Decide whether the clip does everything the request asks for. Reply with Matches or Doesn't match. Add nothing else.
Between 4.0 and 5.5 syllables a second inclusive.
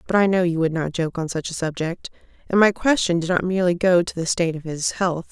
Doesn't match